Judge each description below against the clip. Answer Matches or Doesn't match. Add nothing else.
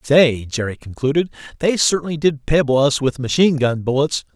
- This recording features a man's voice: Matches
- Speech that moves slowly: Doesn't match